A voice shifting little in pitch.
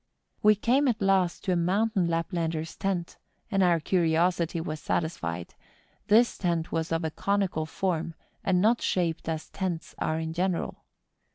No: average, 3.1 semitones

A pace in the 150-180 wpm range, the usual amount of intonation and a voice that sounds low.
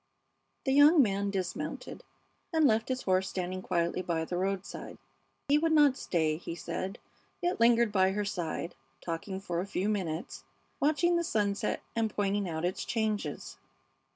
No: average, 155 wpm; average, 4.7 semitones; high, 200 Hz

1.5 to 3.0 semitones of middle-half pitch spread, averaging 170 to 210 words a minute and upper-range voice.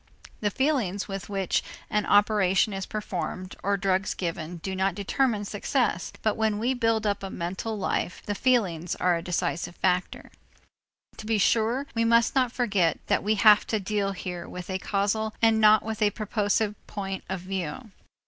Yes: average, 2.7 semitones; average, 175 wpm; high, 205 Hz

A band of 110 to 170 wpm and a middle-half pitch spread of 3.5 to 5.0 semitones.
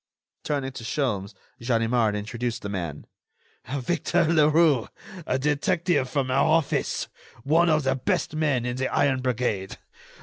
Yes: slow, 135 wpm; average, 4.2 semitones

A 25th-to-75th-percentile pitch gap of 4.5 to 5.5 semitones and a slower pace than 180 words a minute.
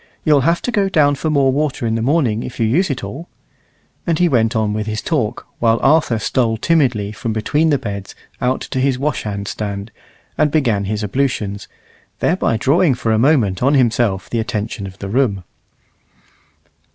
No: average, 5.1 semitones; average, 185 wpm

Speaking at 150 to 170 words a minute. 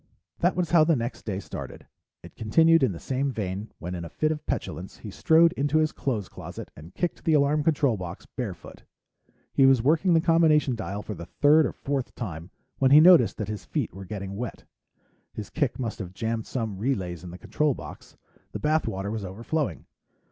No: fast, 205 wpm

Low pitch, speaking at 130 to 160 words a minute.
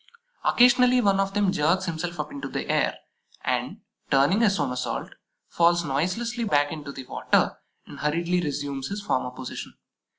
No: medium, 170 Hz; average, 155 wpm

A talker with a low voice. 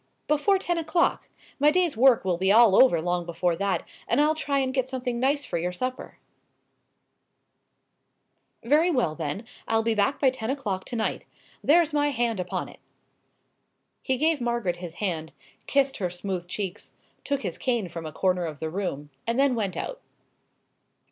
No: high, 230 Hz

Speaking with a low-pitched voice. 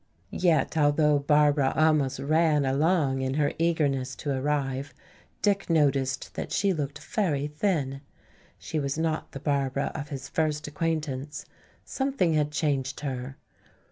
No: medium, 145 Hz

